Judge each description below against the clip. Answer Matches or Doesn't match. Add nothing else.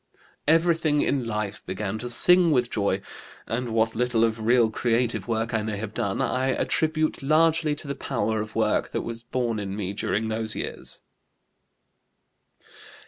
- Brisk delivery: Doesn't match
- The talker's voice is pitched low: Matches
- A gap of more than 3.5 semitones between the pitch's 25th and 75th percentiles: Matches